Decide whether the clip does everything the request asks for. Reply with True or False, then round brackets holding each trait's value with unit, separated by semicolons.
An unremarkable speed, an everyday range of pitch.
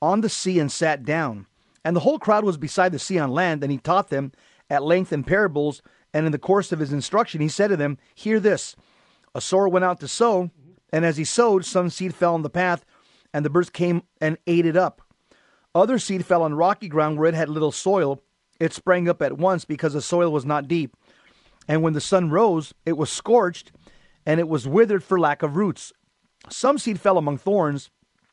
False (220 wpm; 3.8 semitones)